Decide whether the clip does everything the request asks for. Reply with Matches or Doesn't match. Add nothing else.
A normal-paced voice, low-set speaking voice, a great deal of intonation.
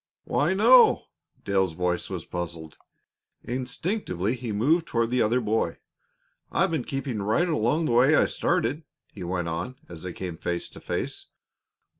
Matches